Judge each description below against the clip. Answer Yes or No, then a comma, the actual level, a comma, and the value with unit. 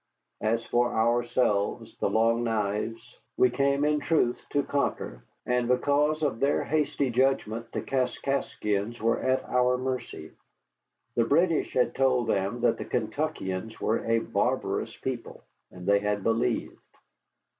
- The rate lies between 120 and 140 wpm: Yes, slow, 135 wpm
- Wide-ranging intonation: No, average, 3.2 semitones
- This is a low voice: Yes, low, 120 Hz